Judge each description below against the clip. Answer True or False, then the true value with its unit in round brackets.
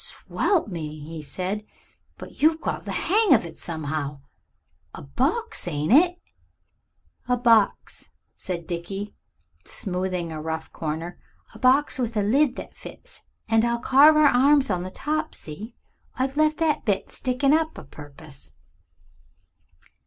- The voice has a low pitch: False (215 Hz)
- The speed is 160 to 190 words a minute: False (145 wpm)